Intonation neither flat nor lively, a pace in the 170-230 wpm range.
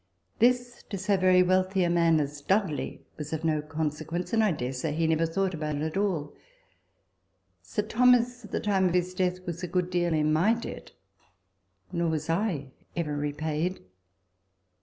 Yes: average, 3.7 semitones; average, 180 wpm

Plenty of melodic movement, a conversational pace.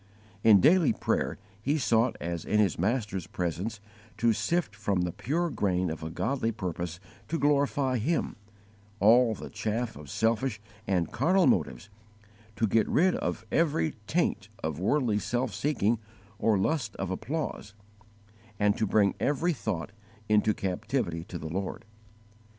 Yes: wide, 6.0 semitones; average, 145 wpm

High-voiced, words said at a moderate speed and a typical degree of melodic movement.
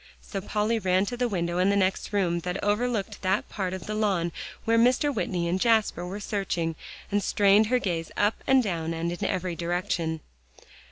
Yes: high, 195 Hz; average, 190 wpm; average, 3.4 semitones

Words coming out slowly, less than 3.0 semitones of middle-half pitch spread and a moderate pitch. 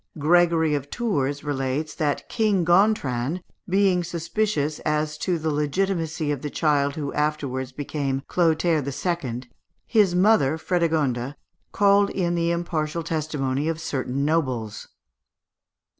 No: slow, 120 wpm; average, 3.5 semitones; medium, 155 Hz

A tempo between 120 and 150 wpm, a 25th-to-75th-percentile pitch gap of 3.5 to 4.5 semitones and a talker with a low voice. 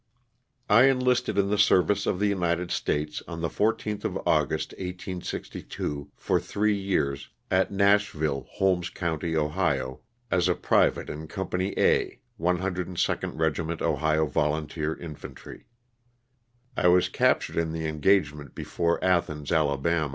Yes: slow, 135 wpm; average, 3.8 semitones; very low, 85 Hz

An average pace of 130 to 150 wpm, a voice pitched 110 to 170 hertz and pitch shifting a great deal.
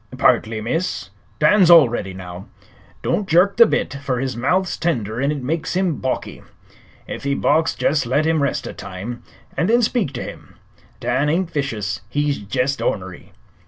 No: average, 165 wpm; medium, 140 Hz; wide, 5.9 semitones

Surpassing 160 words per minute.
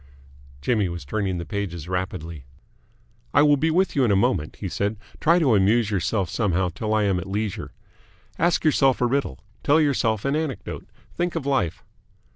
Yes: average, 180 wpm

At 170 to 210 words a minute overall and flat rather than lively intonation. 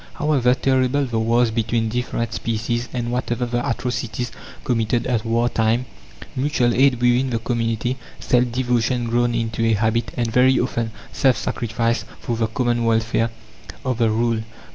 No: average, 155 wpm; narrow, 1.4 semitones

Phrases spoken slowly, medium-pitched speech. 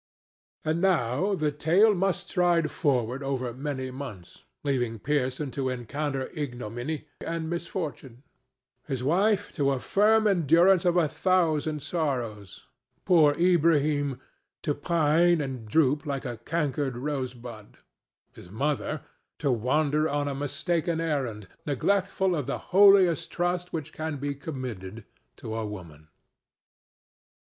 Yes: slow, 125 wpm; medium, 145 Hz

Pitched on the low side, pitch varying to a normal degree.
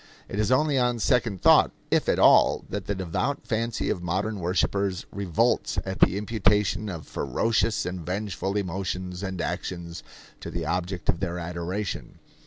Yes: very low, 95 Hz; average, 3.0 semitones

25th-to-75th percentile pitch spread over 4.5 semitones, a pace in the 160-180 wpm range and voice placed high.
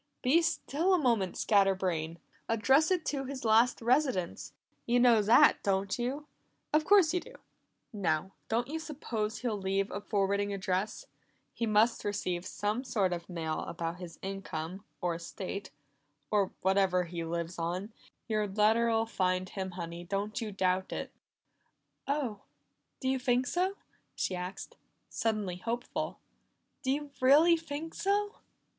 No: wide, 5.6 semitones; average, 145 wpm; high, 210 Hz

